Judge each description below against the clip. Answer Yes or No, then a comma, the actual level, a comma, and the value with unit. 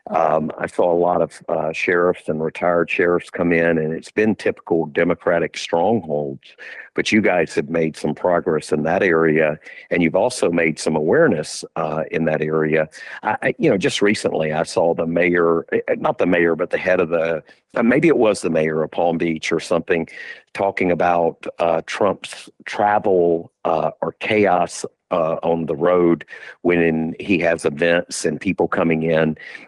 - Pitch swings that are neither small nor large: No, narrow, 1.7 semitones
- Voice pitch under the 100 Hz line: Yes, very low, 85 Hz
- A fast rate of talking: No, average, 175 wpm